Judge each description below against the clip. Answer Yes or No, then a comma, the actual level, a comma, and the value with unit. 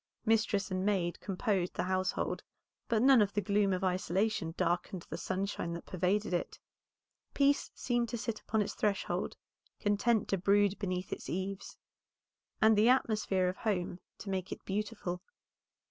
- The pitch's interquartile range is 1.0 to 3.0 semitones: Yes, average, 2.7 semitones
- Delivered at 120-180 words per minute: Yes, average, 155 wpm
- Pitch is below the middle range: No, high, 200 Hz